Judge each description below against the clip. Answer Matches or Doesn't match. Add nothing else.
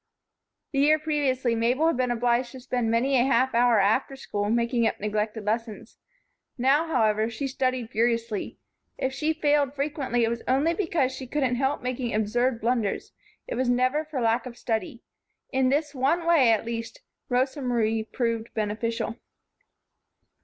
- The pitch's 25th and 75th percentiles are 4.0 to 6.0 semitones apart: Doesn't match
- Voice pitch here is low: Doesn't match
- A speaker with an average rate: Matches